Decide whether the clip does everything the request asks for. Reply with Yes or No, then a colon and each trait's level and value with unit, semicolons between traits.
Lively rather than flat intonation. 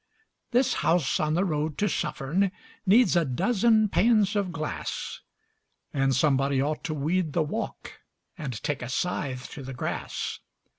Yes: wide, 6.2 semitones